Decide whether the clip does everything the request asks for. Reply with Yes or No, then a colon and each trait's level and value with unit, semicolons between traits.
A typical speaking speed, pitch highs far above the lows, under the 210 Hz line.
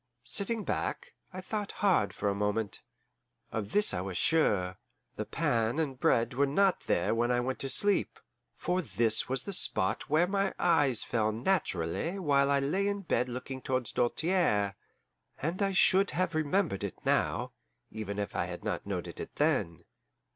Yes: average, 170 wpm; wide, 8.7 semitones; low, 135 Hz